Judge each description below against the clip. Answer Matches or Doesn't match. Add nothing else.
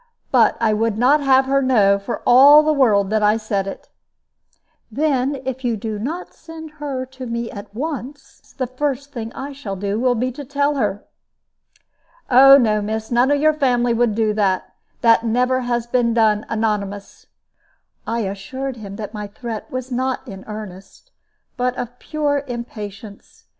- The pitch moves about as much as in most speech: Matches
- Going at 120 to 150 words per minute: Doesn't match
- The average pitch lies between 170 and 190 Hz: Doesn't match